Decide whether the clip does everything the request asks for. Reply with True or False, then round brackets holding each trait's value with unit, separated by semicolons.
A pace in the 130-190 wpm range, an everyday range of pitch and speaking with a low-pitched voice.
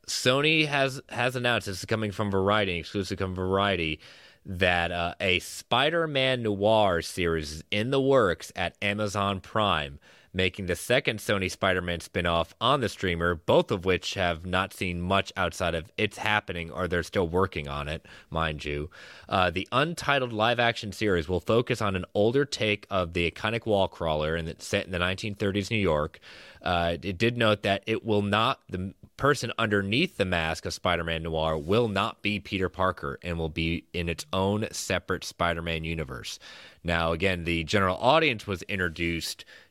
True (180 wpm; 3.9 semitones; 95 Hz)